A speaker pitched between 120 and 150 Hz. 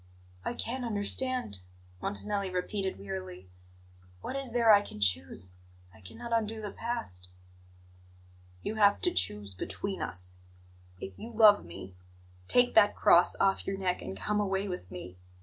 No: high, 195 Hz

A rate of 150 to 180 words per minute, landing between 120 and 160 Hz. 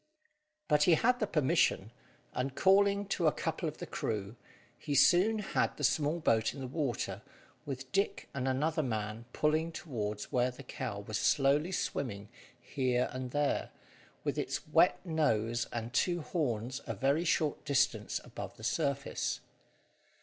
Yes: average, 155 wpm; medium, 140 Hz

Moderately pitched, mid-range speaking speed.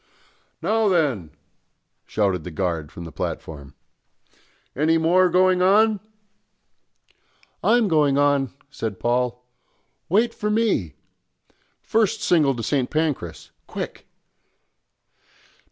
No: medium, 145 Hz; slow, 100 wpm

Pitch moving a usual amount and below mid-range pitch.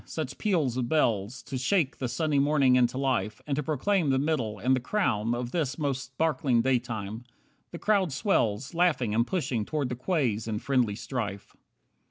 Yes: average, 4.6 semitones; low, 130 Hz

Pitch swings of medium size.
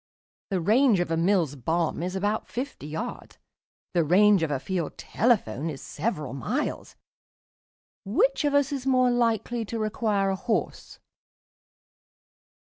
No: wide, 6.4 semitones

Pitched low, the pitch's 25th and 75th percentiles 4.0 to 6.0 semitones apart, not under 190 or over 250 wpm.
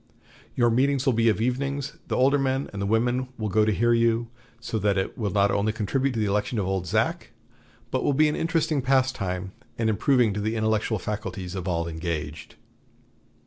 Yes: low, 110 Hz; average, 4.5 semitones; average, 200 wpm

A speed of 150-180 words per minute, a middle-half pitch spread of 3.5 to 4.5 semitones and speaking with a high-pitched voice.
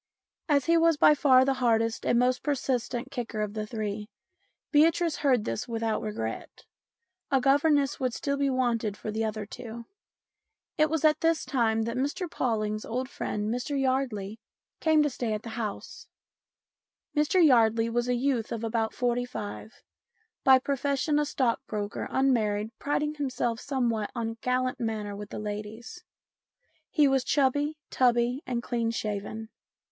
Yes: average, 160 wpm; average, 3.8 semitones; high, 245 Hz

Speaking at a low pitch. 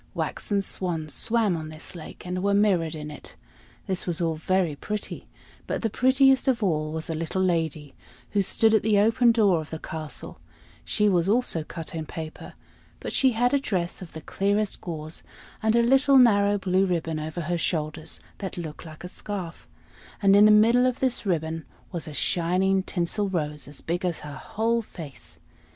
No: medium, 185 Hz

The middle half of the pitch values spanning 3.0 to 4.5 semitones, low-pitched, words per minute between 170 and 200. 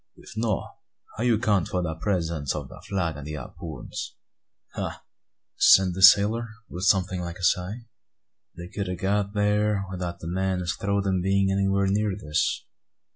No: narrow, 2.6 semitones; very low, 95 Hz; average, 175 wpm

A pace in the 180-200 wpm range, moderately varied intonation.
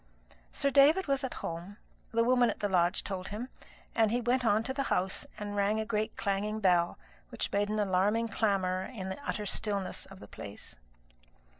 Yes: average, 190 wpm; average, 3.3 semitones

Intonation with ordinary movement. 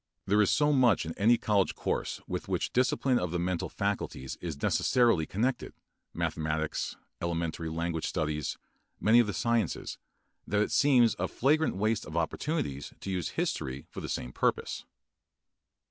No: wide, 6.5 semitones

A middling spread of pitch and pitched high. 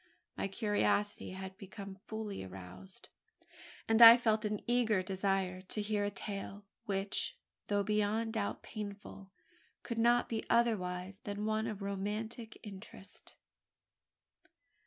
No: narrow, 2.1 semitones; high, 205 Hz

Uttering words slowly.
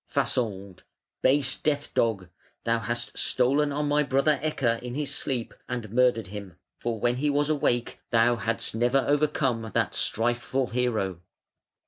No: average, 145 wpm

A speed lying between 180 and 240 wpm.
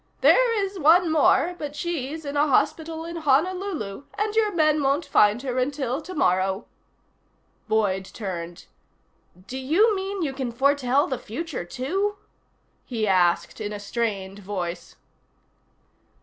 No: slow, 135 wpm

